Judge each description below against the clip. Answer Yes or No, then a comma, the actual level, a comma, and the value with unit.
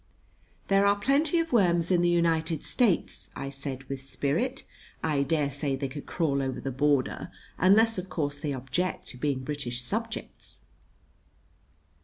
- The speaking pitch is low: No, medium, 150 Hz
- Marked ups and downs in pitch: No, average, 5.0 semitones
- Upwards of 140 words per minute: Yes, average, 155 wpm